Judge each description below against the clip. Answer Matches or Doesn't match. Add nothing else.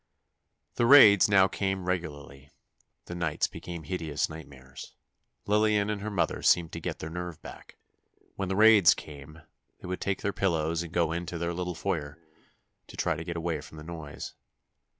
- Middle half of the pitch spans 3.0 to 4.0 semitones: Matches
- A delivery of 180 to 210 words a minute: Doesn't match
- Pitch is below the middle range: Matches